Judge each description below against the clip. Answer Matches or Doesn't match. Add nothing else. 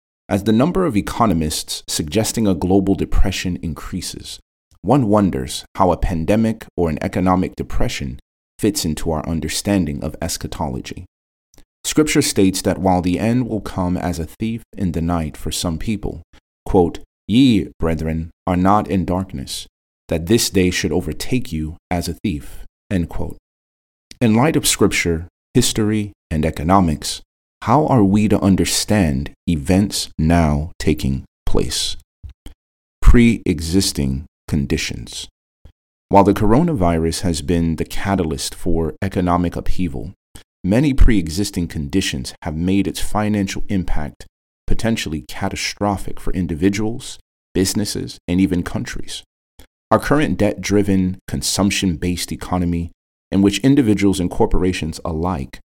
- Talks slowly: Matches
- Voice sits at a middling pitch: Doesn't match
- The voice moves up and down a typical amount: Matches